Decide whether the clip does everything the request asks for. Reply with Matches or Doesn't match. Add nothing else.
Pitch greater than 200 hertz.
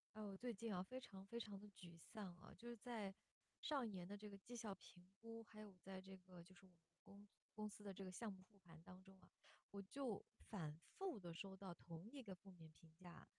Doesn't match